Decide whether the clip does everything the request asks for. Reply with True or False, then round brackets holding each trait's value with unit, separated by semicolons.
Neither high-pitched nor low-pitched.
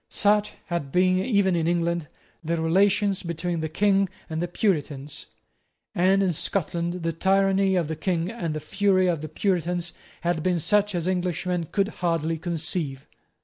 True (175 Hz)